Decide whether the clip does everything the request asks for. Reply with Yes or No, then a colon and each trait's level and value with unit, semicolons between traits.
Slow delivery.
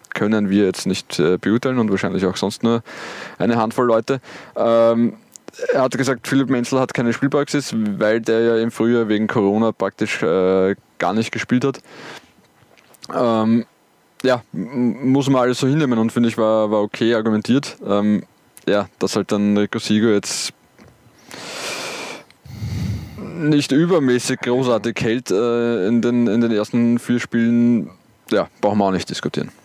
No: average, 155 wpm